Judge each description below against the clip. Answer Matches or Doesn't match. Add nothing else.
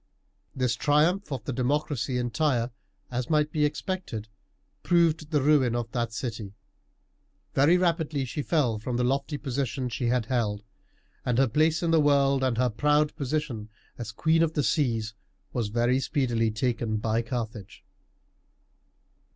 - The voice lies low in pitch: Matches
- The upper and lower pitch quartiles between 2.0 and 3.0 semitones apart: Doesn't match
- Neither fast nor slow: Matches